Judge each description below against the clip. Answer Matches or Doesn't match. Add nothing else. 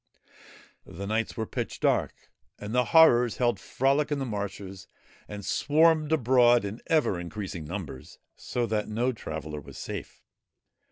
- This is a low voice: Matches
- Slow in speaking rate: Doesn't match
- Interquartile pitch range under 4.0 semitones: Doesn't match